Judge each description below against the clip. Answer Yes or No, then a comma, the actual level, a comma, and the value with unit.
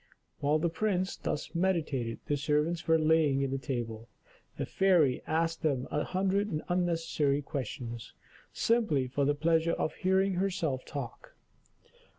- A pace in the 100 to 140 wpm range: Yes, slow, 135 wpm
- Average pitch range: Yes, average, 4.3 semitones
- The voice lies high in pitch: No, medium, 155 Hz